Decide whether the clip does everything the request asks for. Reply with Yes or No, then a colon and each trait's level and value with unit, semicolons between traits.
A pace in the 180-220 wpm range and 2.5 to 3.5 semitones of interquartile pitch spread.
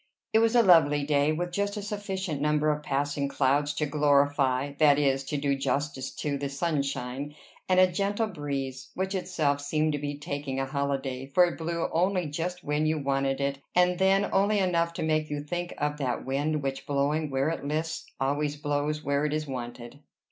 Yes: average, 195 wpm; average, 3.2 semitones